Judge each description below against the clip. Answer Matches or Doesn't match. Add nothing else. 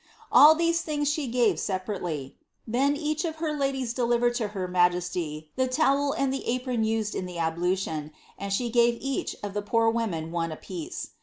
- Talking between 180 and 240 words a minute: Matches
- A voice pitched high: Matches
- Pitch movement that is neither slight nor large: Doesn't match